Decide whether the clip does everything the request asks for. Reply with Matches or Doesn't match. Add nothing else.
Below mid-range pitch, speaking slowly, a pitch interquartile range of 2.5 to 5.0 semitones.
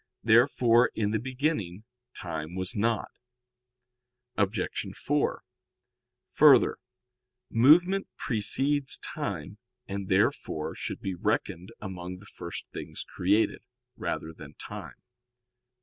Doesn't match